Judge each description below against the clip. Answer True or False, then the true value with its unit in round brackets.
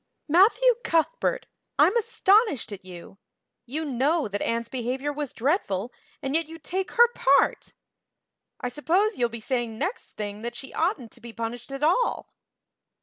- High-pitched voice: True (275 Hz)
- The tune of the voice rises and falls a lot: True (7.4 semitones)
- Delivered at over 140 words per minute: True (155 wpm)